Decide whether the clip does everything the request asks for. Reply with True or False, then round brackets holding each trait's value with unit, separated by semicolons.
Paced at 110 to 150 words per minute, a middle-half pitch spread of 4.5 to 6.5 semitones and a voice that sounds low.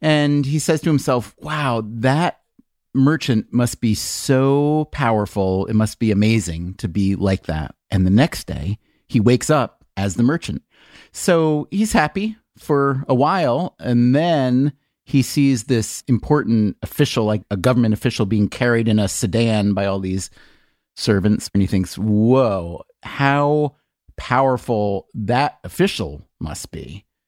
True (145 wpm; 5.6 semitones; 120 Hz)